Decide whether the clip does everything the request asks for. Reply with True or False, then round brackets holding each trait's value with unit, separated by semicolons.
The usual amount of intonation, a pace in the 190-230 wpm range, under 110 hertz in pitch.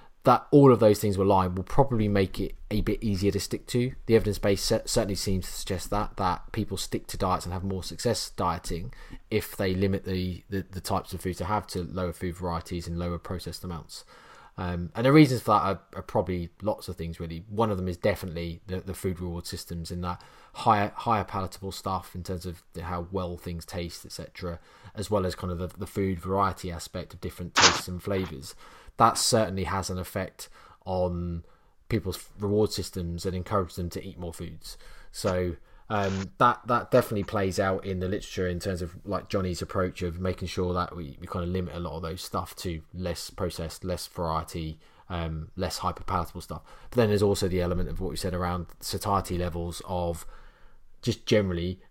False (2.3 semitones; 205 wpm; 95 Hz)